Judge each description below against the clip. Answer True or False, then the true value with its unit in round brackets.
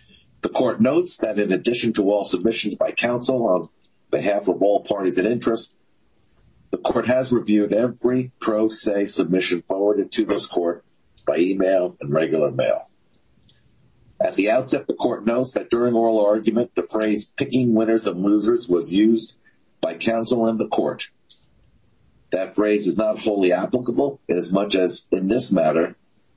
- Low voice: True (110 Hz)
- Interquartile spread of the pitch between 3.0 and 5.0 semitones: False (2.6 semitones)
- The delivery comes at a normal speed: True (160 wpm)